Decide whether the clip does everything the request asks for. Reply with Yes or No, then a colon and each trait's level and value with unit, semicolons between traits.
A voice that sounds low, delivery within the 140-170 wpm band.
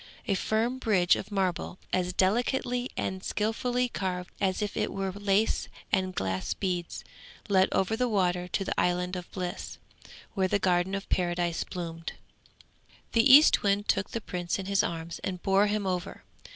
No: high, 190 Hz; average, 165 wpm